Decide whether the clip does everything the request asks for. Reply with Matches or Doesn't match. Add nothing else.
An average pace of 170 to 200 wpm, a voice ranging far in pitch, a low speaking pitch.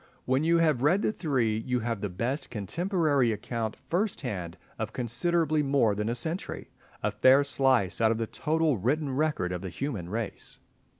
Matches